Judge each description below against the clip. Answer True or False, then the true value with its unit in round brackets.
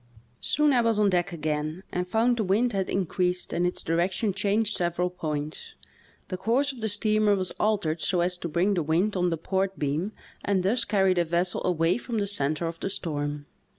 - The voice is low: False (185 Hz)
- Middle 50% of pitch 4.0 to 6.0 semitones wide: False (3.5 semitones)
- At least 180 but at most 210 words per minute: True (205 wpm)